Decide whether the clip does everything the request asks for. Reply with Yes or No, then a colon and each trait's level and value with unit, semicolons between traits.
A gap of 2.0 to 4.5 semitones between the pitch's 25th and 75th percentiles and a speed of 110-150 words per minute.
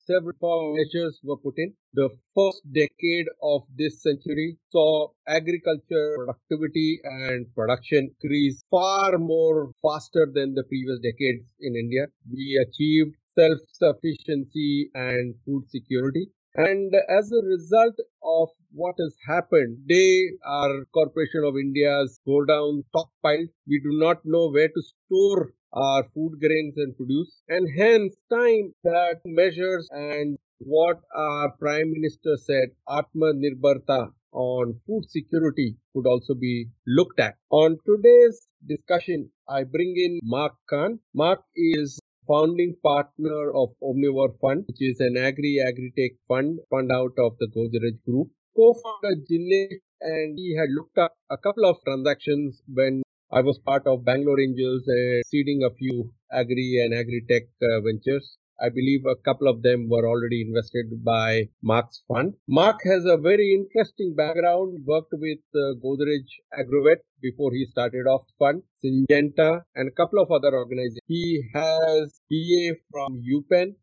Yes: average, 4.1 semitones; average, 145 wpm